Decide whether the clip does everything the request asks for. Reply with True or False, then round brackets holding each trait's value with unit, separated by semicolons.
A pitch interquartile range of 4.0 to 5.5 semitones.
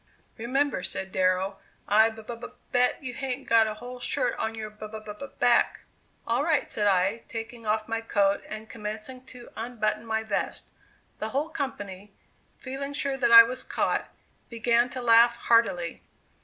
False (2.7 semitones)